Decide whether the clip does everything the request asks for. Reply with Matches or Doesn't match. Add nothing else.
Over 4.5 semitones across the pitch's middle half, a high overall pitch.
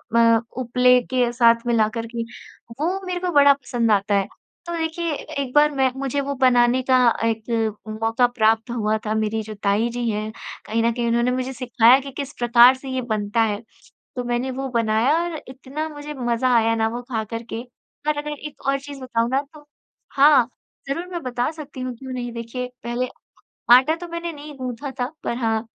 Doesn't match